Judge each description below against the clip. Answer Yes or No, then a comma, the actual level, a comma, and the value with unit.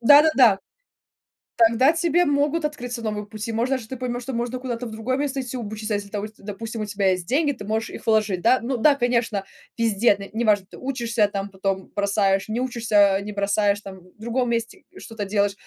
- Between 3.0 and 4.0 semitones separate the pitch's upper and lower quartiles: Yes, average, 3.7 semitones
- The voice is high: Yes, high, 225 Hz